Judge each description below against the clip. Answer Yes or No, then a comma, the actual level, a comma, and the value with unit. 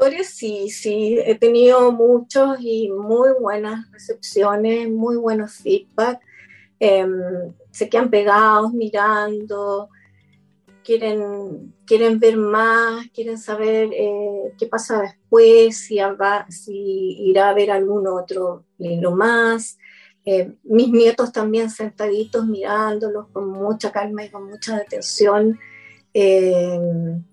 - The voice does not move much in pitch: Yes, narrow, 2.3 semitones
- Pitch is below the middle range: No, high, 215 Hz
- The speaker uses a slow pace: Yes, slow, 110 wpm